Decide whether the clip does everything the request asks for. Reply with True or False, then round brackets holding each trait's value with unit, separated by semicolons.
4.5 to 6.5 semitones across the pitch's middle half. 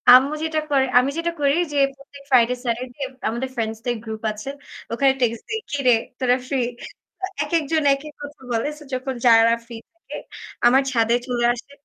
False (3.2 semitones)